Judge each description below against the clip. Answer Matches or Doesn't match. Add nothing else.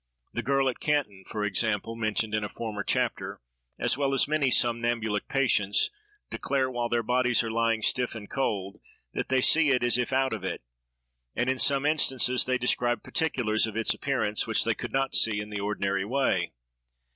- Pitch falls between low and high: Doesn't match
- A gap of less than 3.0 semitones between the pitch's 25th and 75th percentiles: Doesn't match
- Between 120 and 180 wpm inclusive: Doesn't match